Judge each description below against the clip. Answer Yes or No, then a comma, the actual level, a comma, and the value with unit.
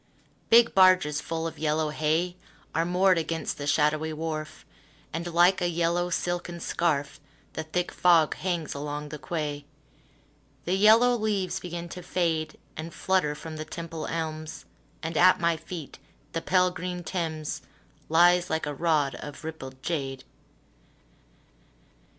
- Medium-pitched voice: Yes, medium, 165 Hz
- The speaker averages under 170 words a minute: Yes, average, 140 wpm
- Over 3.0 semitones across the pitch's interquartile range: No, narrow, 2.4 semitones